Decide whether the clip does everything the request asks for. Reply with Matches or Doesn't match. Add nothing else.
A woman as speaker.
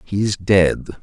Doesn't match